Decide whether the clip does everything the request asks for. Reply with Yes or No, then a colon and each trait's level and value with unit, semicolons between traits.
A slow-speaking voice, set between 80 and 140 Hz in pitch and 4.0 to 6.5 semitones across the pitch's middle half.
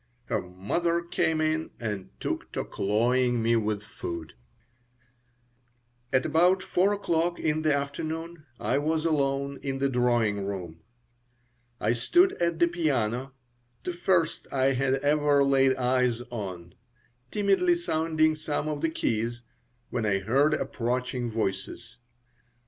Yes: slow, 130 wpm; low, 135 Hz; wide, 5.5 semitones